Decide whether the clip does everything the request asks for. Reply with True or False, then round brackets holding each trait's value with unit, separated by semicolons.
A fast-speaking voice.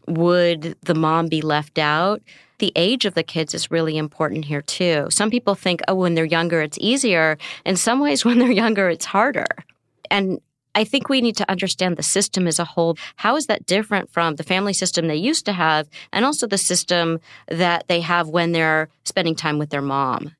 True (210 wpm)